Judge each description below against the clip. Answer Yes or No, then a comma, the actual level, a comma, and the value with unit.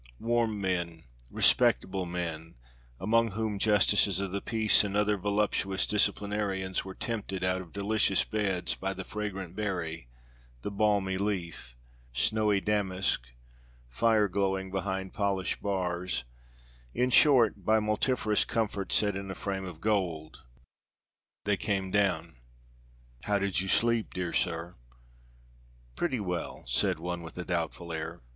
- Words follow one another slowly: Yes, slow, 130 wpm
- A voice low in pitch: Yes, very low, 95 Hz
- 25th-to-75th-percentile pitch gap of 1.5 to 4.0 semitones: Yes, narrow, 2.6 semitones